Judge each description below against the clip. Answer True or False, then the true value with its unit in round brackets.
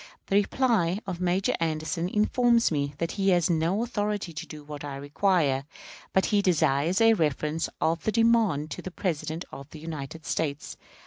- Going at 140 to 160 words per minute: False (175 wpm)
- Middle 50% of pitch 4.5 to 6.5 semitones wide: True (4.9 semitones)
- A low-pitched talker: False (170 Hz)